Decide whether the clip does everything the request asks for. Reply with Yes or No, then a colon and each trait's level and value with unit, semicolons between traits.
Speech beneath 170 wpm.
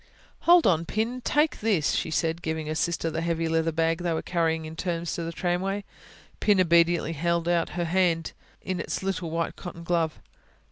No: average, 190 wpm